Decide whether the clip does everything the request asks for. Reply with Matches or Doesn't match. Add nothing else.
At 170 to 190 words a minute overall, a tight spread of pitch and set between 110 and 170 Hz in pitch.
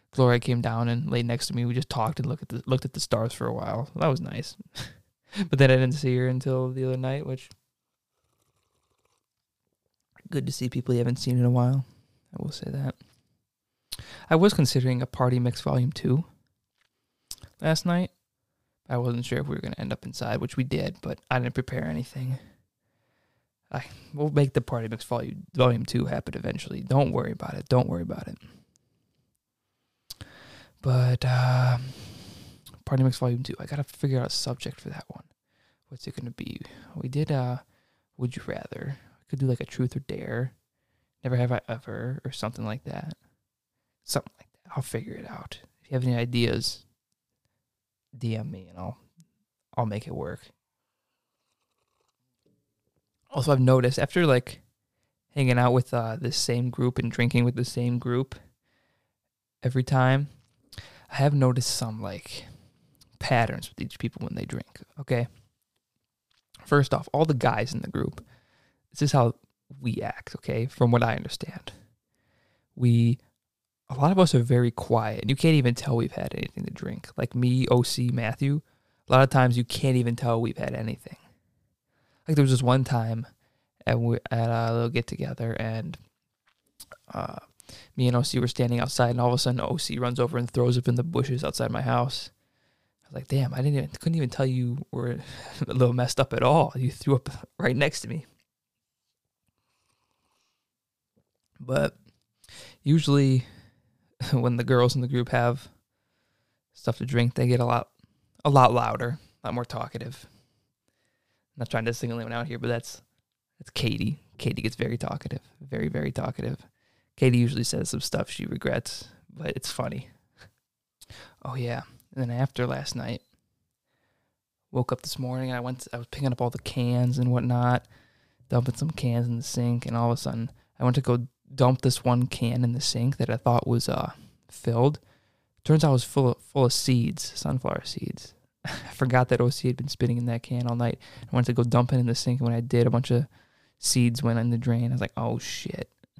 Matches